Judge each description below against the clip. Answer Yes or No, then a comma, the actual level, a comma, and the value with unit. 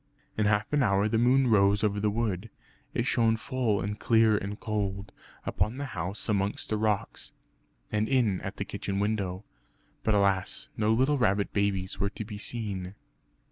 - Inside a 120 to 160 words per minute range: No, average, 175 wpm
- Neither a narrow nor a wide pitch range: No, narrow, 2.1 semitones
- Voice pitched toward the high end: No, low, 105 Hz